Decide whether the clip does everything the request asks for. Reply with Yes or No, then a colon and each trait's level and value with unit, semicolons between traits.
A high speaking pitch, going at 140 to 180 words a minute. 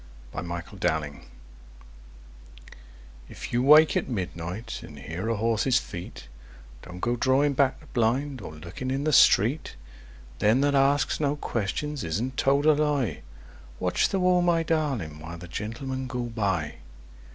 No: low, 120 Hz; average, 150 wpm